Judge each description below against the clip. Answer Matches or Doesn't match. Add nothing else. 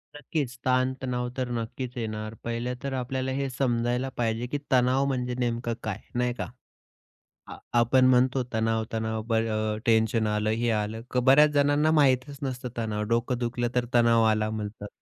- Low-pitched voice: Matches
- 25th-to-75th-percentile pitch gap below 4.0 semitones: Matches